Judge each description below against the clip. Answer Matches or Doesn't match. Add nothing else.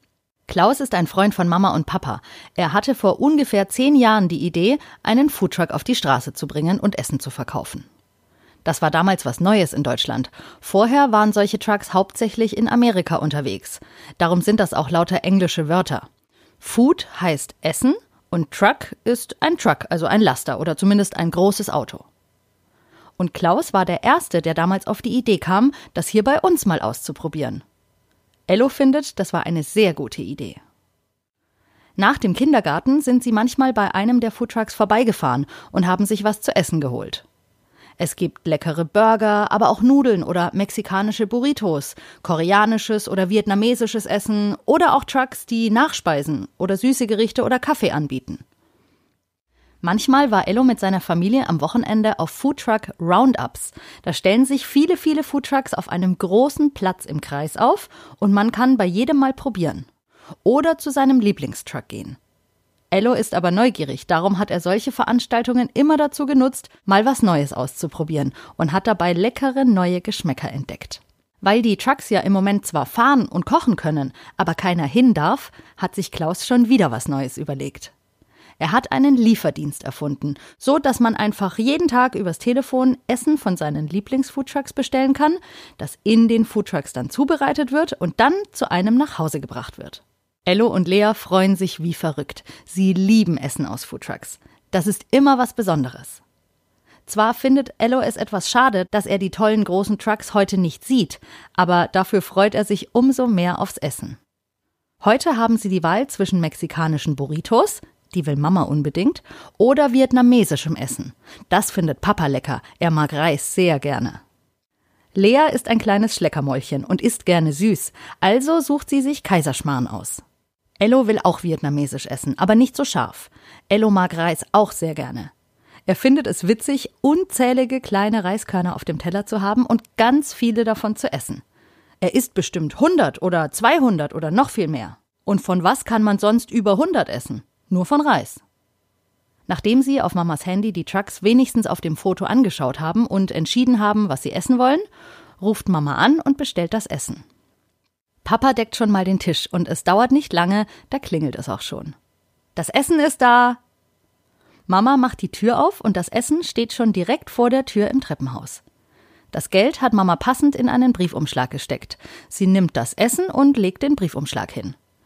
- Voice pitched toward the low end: Doesn't match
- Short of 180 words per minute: Matches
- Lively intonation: Matches